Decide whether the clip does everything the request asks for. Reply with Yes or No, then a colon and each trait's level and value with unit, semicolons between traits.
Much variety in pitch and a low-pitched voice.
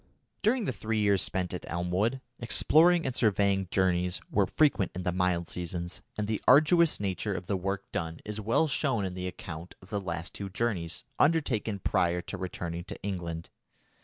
No: average, 4.3 semitones; very low, 95 Hz